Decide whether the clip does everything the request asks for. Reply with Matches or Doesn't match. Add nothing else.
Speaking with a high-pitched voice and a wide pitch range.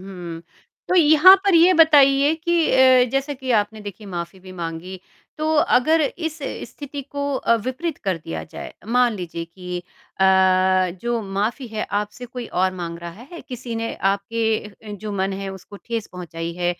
Matches